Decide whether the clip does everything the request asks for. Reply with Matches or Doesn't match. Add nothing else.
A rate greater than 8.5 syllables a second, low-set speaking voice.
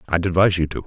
Matches